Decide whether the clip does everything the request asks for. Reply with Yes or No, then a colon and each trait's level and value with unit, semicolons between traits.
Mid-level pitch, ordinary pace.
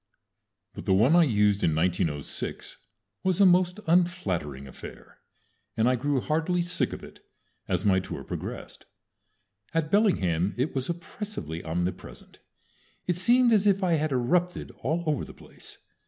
Yes: medium, 150 Hz; average, 150 wpm